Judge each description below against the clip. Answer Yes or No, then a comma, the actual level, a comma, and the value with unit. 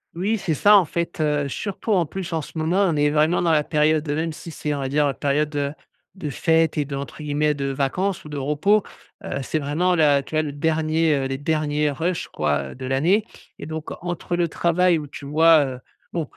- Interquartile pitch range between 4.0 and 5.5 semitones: No, average, 2.8 semitones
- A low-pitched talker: No, medium, 155 Hz